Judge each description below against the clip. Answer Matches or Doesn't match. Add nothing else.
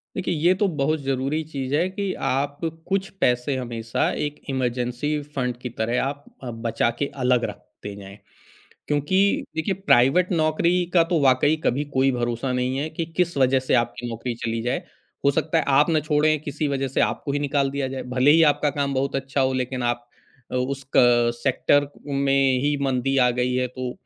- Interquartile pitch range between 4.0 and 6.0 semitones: Doesn't match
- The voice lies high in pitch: Doesn't match